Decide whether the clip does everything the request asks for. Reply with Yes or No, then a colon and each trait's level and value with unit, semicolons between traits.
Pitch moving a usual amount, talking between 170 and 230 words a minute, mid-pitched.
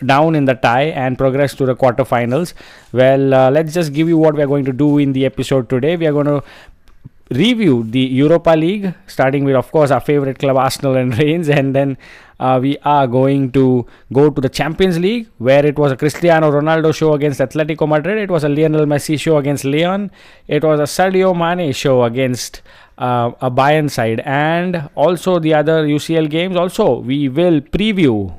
Yes: average, 3.3 semitones; average, 200 wpm; medium, 145 Hz